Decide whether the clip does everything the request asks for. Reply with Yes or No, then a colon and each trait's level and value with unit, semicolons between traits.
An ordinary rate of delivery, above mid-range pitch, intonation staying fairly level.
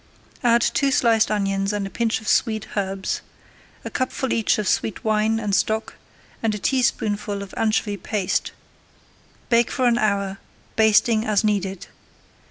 Yes: average, 150 wpm; high, 215 Hz; narrow, 2.2 semitones